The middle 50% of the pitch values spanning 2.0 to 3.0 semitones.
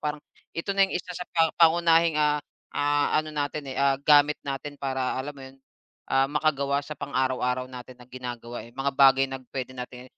Yes: narrow, 2.5 semitones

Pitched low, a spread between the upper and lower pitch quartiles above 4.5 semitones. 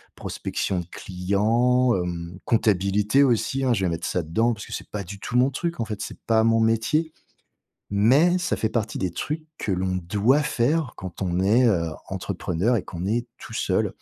Yes: low, 110 Hz; average, 5.0 semitones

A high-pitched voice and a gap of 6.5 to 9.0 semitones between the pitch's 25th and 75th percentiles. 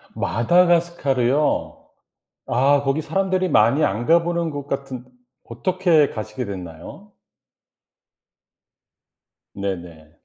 No: medium, 140 Hz; wide, 7.0 semitones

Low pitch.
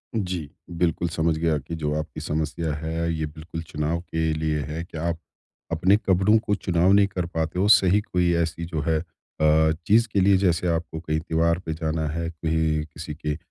Yes: very low, 80 Hz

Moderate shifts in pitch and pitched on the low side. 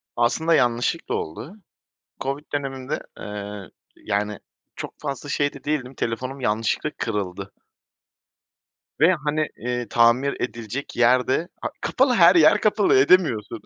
Yes: average, 4.8 semitones; low, 130 Hz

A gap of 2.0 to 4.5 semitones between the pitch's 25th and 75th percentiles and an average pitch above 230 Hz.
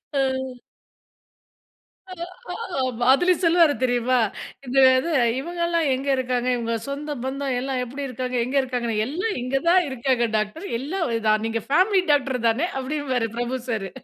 Yes: average, 3.4 semitones; very high, 260 Hz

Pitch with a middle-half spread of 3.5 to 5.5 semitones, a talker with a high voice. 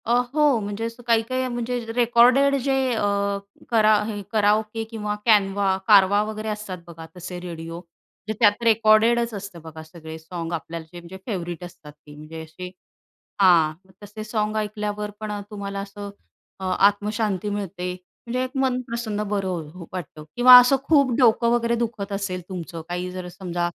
Yes: average, 4.1 semitones; high, 205 Hz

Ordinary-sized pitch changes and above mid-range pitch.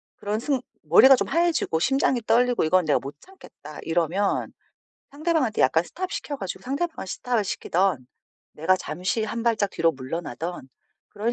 No: wide, 8.1 semitones; high, 210 Hz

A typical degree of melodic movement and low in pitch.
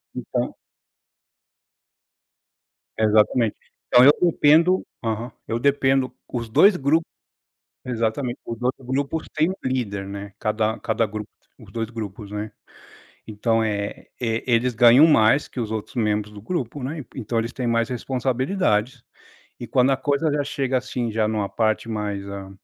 Yes: average, 3.6 semitones; low, 115 Hz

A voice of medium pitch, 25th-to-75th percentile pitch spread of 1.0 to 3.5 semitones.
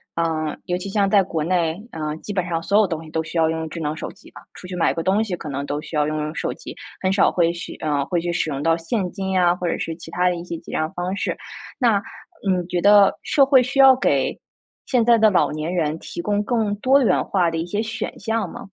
No: medium, 180 Hz; average, 4.0 semitones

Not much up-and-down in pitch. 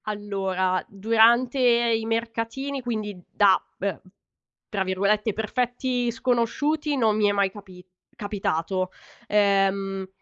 No: average, 3.4 semitones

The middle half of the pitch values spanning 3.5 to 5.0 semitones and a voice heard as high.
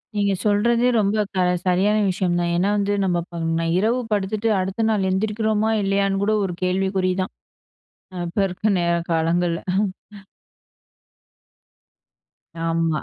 No: average, 3.0 semitones; high, 195 Hz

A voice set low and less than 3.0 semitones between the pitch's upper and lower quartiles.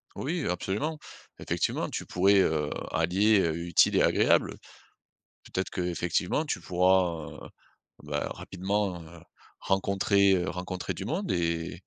Yes: very low, 95 Hz; narrow, 2.5 semitones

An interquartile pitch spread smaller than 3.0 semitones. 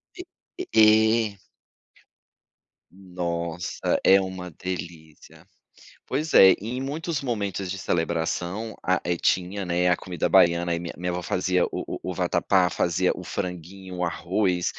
Yes: narrow, 2.5 semitones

